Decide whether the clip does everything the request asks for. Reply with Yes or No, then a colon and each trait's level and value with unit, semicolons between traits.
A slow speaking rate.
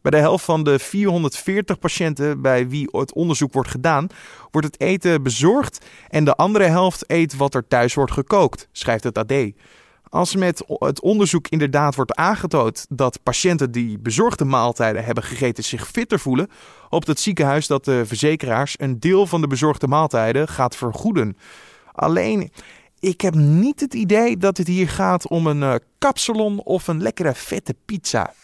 No: average, 165 wpm